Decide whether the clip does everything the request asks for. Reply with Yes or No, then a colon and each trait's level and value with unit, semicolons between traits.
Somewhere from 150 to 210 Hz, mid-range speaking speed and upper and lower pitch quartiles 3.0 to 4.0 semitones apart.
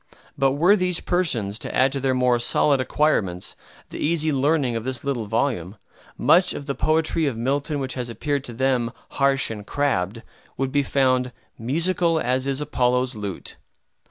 No: low, 135 Hz; average, 170 wpm; average, 3.4 semitones